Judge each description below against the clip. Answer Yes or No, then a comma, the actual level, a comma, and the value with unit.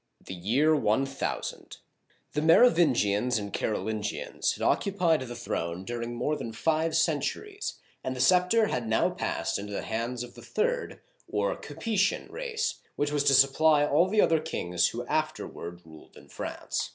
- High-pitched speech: No, medium, 140 Hz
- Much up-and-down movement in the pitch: Yes, wide, 7.2 semitones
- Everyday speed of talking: Yes, average, 165 wpm